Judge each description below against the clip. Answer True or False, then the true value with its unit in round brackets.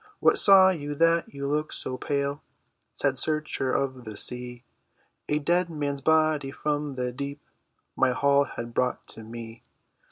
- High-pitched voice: False (140 Hz)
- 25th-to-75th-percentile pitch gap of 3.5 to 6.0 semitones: False (3.1 semitones)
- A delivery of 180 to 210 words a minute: False (155 wpm)